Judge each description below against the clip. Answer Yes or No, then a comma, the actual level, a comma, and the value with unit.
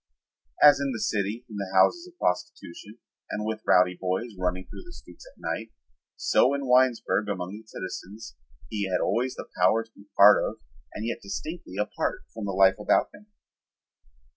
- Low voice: Yes, low, 105 Hz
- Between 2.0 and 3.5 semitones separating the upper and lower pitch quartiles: No, average, 4.8 semitones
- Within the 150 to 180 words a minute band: No, average, 190 wpm